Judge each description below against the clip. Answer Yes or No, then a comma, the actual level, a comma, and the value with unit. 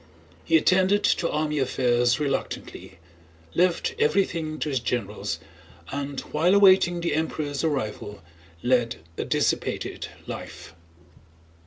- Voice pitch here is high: No, medium, 150 Hz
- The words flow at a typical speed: No, slow, 110 wpm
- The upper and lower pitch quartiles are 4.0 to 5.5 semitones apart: Yes, average, 5.1 semitones